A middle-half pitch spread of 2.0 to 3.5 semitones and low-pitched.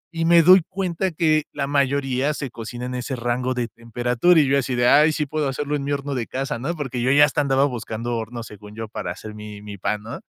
No: average, 3.9 semitones; low, 130 Hz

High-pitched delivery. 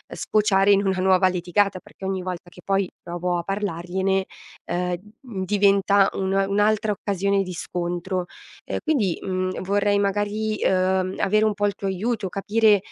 Yes: high, 195 Hz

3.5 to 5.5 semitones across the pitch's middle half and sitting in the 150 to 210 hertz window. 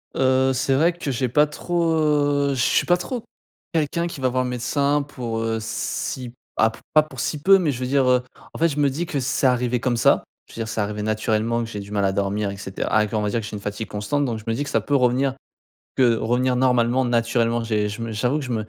No: average, 4.0 semitones; low, 125 Hz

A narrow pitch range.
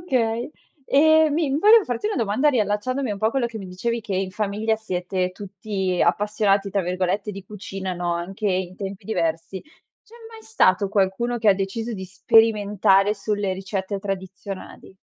No: average, 3.0 semitones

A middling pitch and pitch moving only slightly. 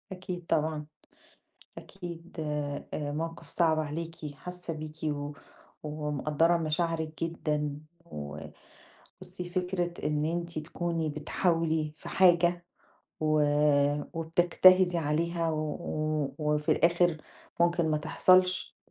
Yes: medium, 165 Hz; narrow, 2.3 semitones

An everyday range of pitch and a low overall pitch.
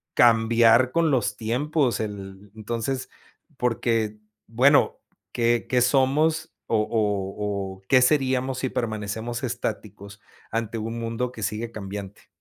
Yes: average, 3.0 semitones; low, 115 Hz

